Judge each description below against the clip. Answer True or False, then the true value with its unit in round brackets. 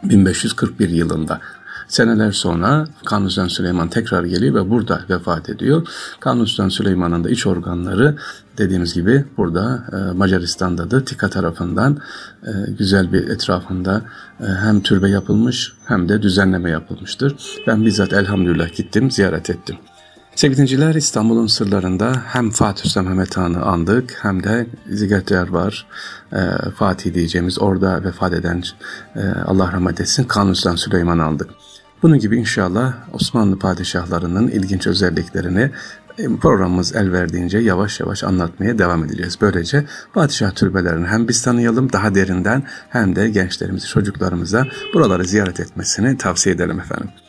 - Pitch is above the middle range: False (100 Hz)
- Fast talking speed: False (125 wpm)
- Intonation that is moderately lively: True (3.8 semitones)